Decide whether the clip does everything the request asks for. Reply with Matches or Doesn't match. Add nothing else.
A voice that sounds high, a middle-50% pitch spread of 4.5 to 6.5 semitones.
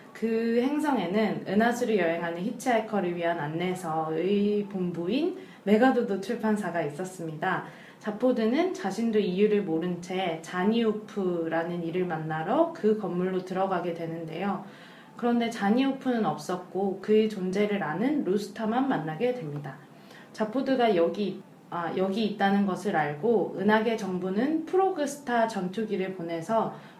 Doesn't match